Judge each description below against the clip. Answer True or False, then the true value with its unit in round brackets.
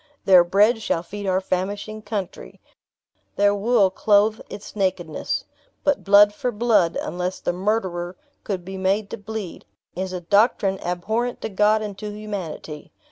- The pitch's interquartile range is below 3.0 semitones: True (2.5 semitones)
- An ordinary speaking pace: True (150 wpm)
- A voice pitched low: False (200 Hz)